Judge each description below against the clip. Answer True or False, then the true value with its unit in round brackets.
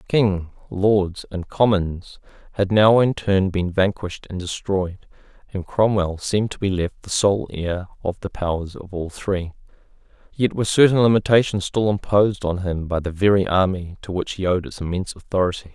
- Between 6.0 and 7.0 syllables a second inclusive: False (4.9 syllables/s)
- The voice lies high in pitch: False (95 Hz)